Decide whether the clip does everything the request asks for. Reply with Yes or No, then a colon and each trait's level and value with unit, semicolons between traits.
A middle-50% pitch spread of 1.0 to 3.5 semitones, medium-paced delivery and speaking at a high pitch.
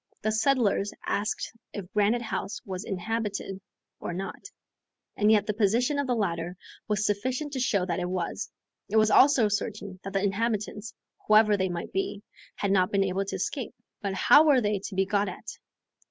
Yes: narrow, 2.4 semitones; average, 185 wpm; high, 205 Hz